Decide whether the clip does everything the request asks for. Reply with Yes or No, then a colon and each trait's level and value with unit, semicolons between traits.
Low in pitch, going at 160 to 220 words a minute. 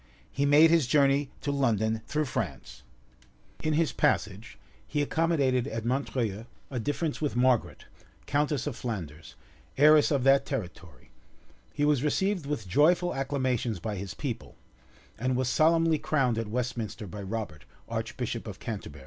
No: low, 130 Hz; average, 145 wpm